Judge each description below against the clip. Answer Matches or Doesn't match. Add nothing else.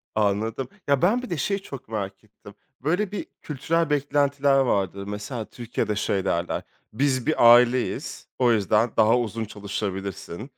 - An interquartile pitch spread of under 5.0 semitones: Doesn't match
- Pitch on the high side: Doesn't match